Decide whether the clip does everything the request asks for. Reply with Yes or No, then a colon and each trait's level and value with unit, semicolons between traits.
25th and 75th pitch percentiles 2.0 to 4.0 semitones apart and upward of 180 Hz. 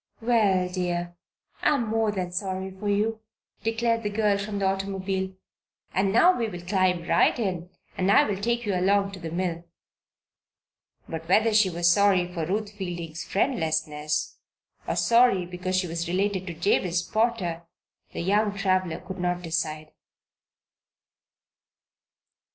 Yes: average, 2.9 semitones; high, 190 Hz